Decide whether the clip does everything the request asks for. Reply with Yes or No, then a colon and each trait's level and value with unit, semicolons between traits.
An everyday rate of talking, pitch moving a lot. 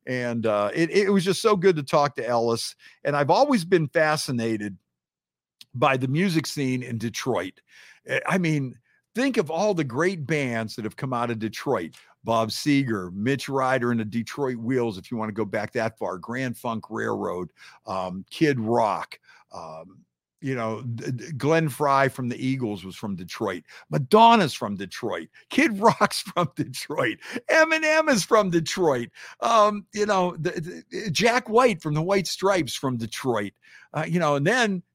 Yes: average, 170 wpm; wide, 7.8 semitones